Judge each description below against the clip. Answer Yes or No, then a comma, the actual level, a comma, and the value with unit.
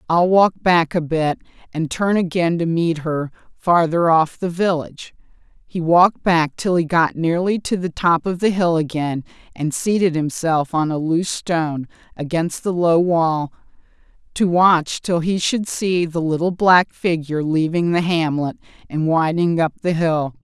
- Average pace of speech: Yes, average, 170 wpm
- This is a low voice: No, medium, 165 Hz